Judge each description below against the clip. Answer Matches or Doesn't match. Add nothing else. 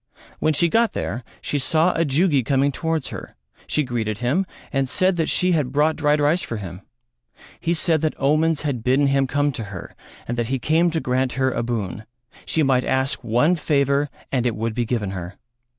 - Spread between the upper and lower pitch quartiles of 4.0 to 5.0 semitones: Matches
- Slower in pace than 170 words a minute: Doesn't match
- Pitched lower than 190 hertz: Matches